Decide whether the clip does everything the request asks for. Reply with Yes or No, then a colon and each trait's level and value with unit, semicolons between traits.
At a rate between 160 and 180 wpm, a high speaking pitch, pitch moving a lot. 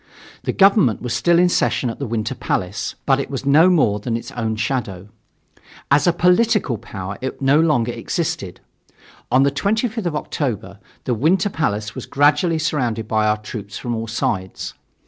No: average, 175 wpm; low, 130 Hz; wide, 6.7 semitones